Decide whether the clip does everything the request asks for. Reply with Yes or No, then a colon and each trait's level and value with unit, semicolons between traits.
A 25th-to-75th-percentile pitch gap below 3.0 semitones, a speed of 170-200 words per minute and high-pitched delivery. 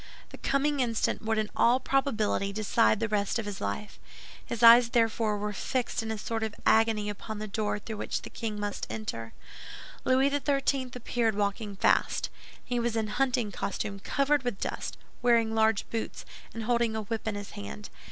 Yes: narrow, 2.5 semitones; average, 180 wpm; high, 220 Hz